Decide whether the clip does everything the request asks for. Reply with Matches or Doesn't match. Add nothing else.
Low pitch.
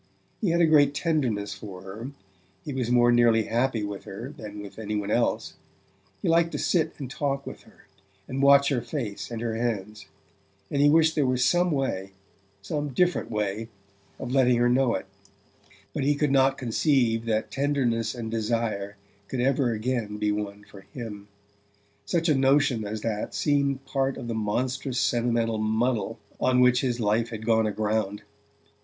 Matches